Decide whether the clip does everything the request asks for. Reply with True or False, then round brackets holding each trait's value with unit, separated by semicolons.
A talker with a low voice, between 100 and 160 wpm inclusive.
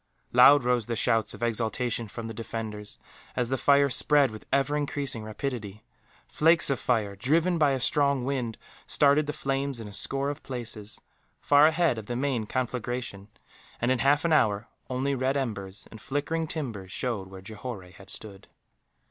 False (125 Hz; 175 wpm)